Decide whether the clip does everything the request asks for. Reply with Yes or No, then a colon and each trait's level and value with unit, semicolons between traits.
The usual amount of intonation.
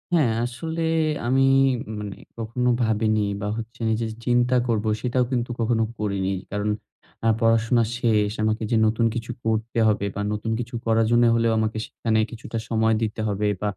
No: narrow, 1.7 semitones